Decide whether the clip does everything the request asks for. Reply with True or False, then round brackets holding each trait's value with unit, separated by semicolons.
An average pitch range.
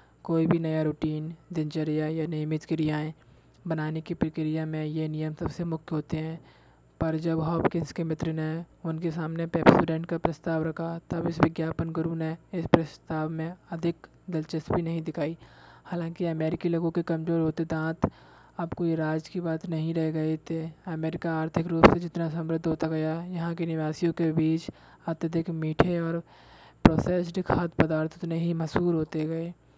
False (1.1 semitones)